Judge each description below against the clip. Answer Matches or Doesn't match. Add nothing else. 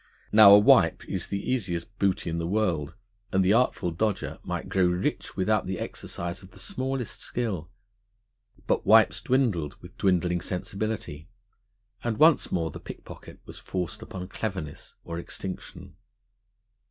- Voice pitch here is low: Matches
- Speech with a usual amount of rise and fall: Matches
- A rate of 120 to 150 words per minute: Matches